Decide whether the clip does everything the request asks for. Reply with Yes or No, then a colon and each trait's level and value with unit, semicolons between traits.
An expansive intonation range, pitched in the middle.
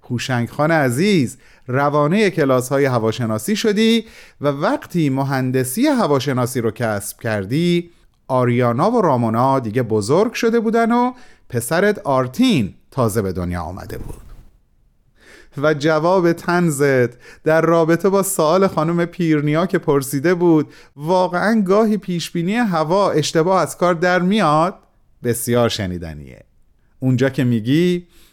Yes: wide, 6.4 semitones; medium, 155 Hz